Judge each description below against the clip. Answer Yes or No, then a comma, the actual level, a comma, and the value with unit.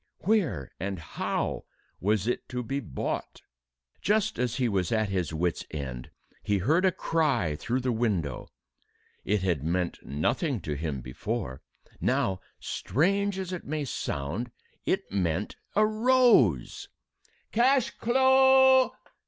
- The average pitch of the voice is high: No, low, 115 Hz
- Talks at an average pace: No, slow, 130 wpm